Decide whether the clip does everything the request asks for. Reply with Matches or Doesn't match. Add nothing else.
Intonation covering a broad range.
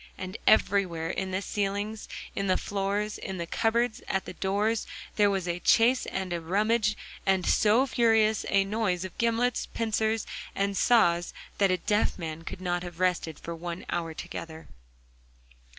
Doesn't match